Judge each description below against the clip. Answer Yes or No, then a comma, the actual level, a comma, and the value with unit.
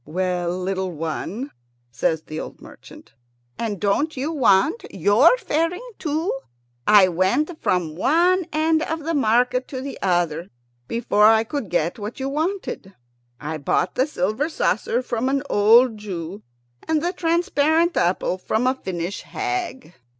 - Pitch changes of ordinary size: No, wide, 8.8 semitones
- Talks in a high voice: Yes, high, 230 Hz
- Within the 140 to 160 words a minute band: Yes, average, 145 wpm